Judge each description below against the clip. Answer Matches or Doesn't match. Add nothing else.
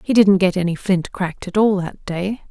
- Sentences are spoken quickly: Matches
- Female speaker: Matches